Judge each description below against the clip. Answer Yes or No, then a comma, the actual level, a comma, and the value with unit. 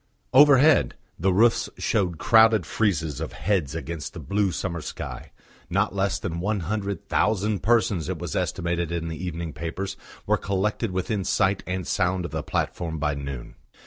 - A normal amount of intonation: Yes, average, 3.7 semitones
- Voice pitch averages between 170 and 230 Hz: No, very low, 95 Hz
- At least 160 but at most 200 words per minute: Yes, average, 165 wpm